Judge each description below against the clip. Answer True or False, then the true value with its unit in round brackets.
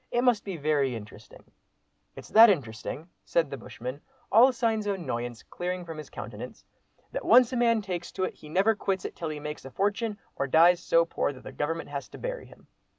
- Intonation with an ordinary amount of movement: False (6.9 semitones)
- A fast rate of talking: True (215 wpm)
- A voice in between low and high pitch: True (170 Hz)